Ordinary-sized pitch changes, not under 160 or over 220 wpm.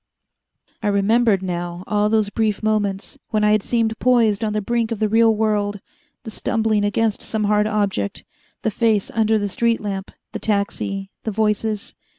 No: narrow, 1.5 semitones; average, 170 wpm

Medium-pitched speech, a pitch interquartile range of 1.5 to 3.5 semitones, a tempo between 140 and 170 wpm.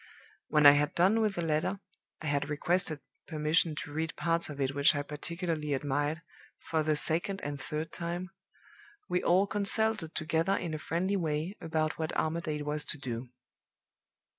Yes: medium, 155 Hz; average, 2.7 semitones; average, 165 wpm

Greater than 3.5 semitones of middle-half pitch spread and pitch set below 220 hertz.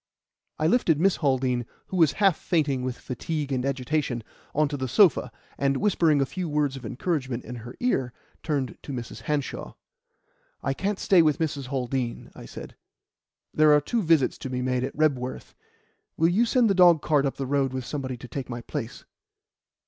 Yes: average, 3.9 semitones; medium, 140 Hz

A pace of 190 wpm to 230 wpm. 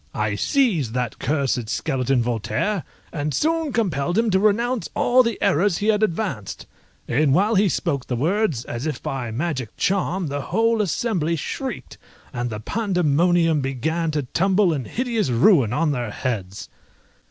No: average, 155 wpm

